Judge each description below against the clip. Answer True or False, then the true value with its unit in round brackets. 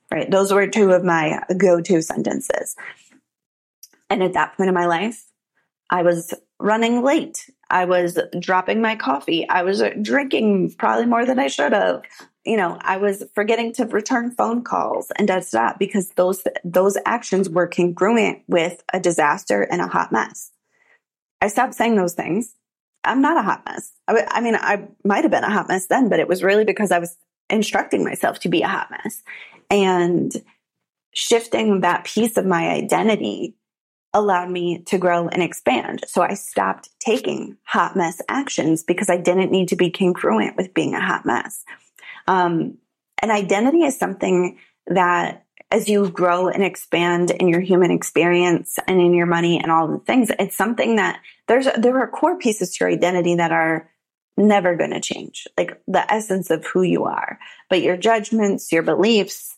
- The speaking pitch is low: False (190 Hz)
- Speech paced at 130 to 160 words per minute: False (180 wpm)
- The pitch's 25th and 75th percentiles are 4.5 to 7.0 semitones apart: False (3.9 semitones)